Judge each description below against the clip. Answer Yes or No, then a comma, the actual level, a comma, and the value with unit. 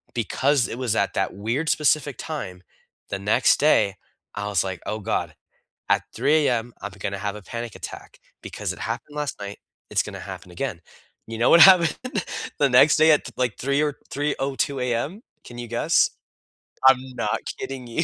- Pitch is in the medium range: No, low, 120 Hz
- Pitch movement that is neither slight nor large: No, wide, 5.9 semitones